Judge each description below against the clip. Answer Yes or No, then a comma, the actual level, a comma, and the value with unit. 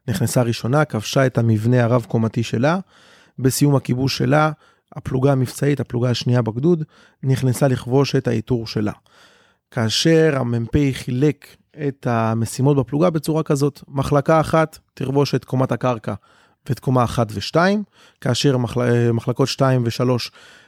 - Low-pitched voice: Yes, low, 130 Hz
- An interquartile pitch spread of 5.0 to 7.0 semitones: No, average, 3.2 semitones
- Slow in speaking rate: No, average, 125 wpm